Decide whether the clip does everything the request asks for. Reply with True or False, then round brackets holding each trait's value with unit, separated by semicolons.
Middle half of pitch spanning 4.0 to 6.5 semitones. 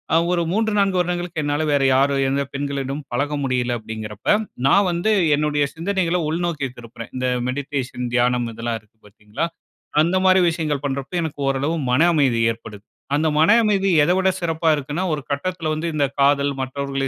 True (4.5 semitones)